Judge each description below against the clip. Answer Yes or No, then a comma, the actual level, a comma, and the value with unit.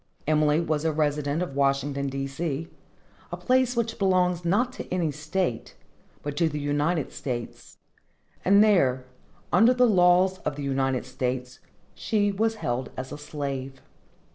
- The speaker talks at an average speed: Yes, average, 150 wpm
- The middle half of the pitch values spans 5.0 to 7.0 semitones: Yes, average, 5.3 semitones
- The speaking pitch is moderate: Yes, medium, 150 Hz